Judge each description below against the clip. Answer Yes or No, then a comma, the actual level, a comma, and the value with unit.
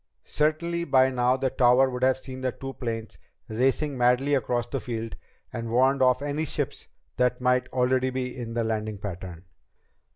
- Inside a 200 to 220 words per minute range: No, average, 170 wpm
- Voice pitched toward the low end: Yes, low, 125 Hz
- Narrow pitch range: Yes, narrow, 1.9 semitones